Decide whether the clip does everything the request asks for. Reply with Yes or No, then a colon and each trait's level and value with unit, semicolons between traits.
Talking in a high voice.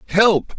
Yes: high, 195 Hz